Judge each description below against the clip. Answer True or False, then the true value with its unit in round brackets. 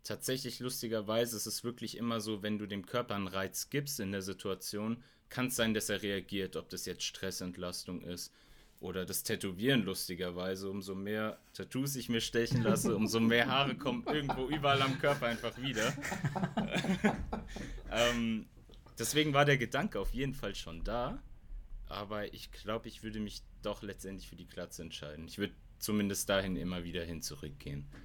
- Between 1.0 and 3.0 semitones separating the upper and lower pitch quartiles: False (4.1 semitones)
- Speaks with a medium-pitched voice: False (105 Hz)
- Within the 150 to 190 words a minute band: True (170 wpm)